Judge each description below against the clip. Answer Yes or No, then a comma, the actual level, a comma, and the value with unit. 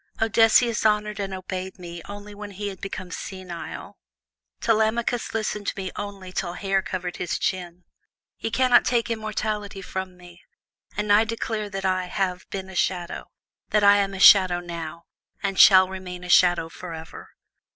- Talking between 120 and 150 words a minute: No, average, 160 wpm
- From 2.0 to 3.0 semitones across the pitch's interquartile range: Yes, narrow, 2.6 semitones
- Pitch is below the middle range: No, high, 195 Hz